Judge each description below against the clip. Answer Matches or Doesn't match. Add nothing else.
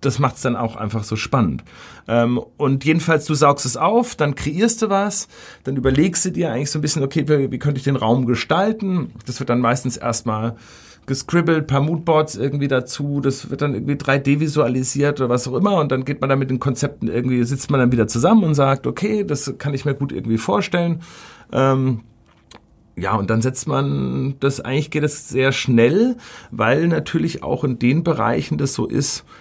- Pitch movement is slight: Doesn't match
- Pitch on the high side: Doesn't match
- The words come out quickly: Matches